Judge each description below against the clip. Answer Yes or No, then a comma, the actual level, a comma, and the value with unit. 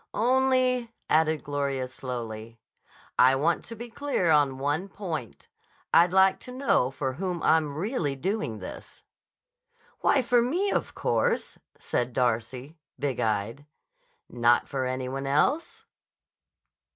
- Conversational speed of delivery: No, slow, 125 wpm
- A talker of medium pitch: Yes, medium, 145 Hz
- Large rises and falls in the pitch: Yes, wide, 8.2 semitones